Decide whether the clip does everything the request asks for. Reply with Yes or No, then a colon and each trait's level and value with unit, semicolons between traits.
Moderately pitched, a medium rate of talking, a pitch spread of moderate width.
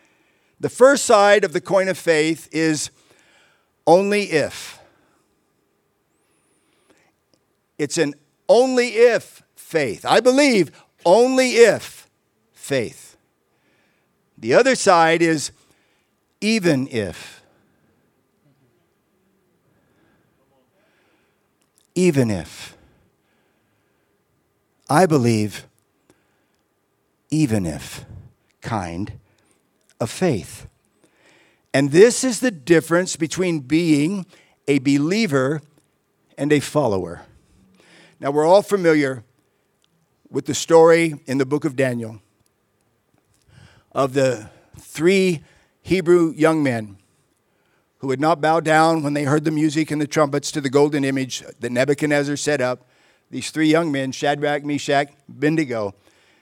No: medium, 150 Hz; slow, 100 wpm; average, 4.0 semitones